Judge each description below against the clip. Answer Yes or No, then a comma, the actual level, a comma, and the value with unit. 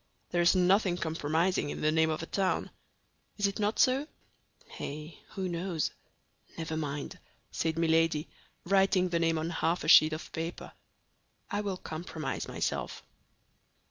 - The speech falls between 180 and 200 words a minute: No, average, 145 wpm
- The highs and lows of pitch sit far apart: No, average, 2.8 semitones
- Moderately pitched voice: Yes, medium, 165 Hz